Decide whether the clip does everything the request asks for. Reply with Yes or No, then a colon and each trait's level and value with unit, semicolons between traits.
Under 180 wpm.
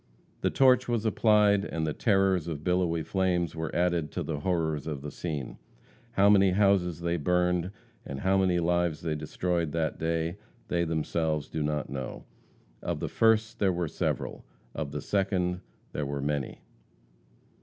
Yes: average, 165 wpm